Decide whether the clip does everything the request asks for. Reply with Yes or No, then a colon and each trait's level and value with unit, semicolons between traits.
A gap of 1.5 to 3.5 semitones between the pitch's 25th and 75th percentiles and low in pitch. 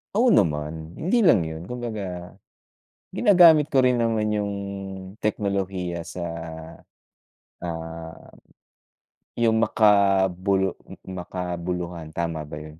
No: average, 4.8 semitones; very low, 95 Hz